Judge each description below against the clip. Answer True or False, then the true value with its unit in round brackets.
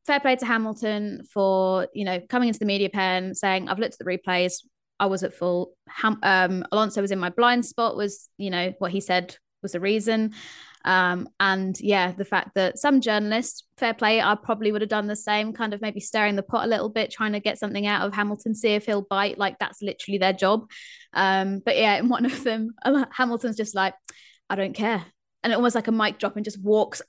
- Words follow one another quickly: True (230 wpm)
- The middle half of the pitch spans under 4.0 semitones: True (2.7 semitones)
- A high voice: True (210 Hz)